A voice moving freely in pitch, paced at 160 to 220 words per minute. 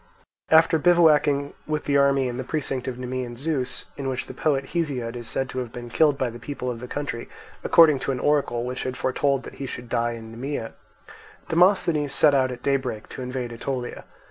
No: average, 2.9 semitones; fast, 205 wpm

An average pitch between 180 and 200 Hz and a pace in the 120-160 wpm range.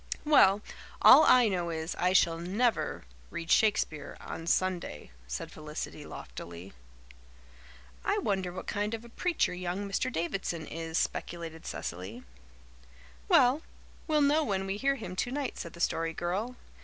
Yes: medium, 185 Hz; average, 145 wpm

